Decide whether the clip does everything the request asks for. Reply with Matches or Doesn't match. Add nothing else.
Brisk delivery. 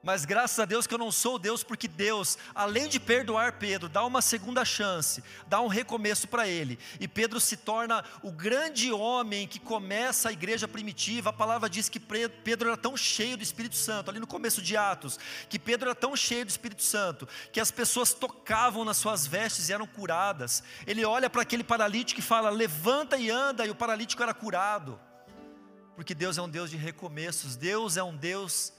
Matches